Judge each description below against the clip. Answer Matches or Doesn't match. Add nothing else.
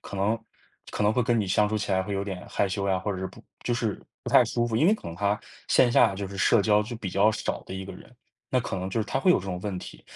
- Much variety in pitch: Doesn't match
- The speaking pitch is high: Doesn't match